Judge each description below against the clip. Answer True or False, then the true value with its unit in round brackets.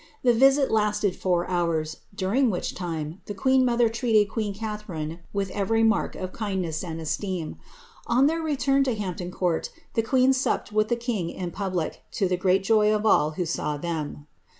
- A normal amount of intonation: True (4.5 semitones)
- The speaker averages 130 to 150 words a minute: False (180 wpm)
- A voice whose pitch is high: True (200 Hz)